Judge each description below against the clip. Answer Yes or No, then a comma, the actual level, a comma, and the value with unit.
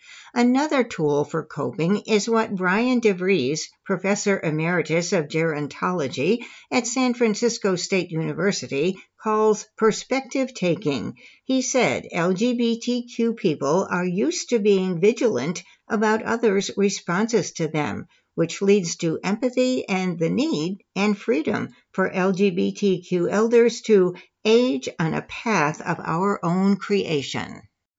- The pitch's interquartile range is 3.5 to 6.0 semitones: Yes, average, 4.5 semitones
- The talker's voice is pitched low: No, high, 200 Hz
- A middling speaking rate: No, slow, 120 wpm